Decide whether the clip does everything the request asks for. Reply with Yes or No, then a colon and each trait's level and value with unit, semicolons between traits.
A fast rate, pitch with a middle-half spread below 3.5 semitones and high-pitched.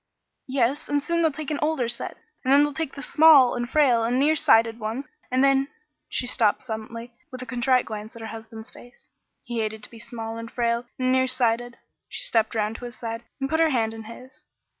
Yes: fast, 225 wpm; average, 3.1 semitones; high, 245 Hz